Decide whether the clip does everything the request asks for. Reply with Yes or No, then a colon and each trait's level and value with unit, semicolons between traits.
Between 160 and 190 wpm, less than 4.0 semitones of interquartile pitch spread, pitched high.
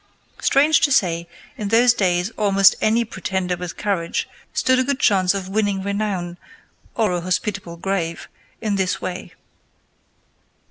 No: average, 140 wpm; average, 3.2 semitones; high, 195 Hz